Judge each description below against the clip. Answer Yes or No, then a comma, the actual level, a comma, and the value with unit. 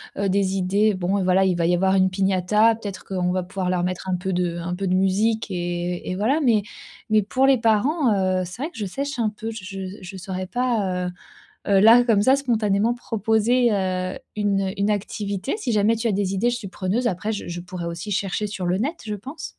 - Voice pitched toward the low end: No, high, 195 Hz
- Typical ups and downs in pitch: Yes, average, 3.2 semitones